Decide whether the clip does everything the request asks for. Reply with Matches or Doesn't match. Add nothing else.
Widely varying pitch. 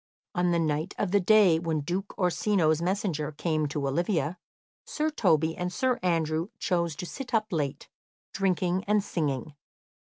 Doesn't match